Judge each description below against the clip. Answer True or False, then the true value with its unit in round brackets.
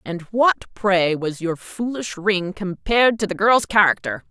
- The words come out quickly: False (165 wpm)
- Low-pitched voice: False (195 Hz)